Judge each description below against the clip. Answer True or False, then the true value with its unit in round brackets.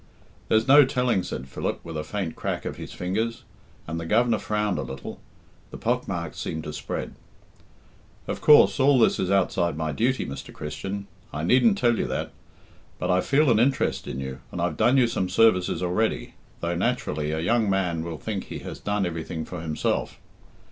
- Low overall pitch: True (95 Hz)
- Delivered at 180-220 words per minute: True (190 wpm)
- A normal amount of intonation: False (6.3 semitones)